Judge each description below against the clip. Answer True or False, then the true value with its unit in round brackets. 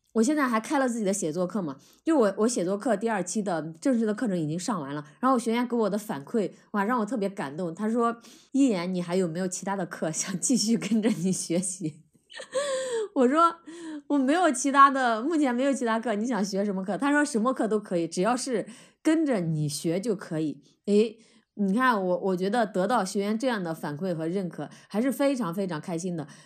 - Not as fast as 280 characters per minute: False (310 characters per minute)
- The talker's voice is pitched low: False (215 Hz)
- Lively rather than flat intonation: True (5.7 semitones)